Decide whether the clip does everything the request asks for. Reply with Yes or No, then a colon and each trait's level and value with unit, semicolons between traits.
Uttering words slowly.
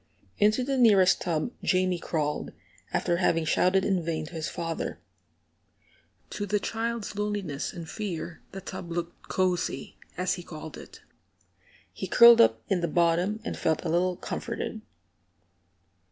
No: average, 145 wpm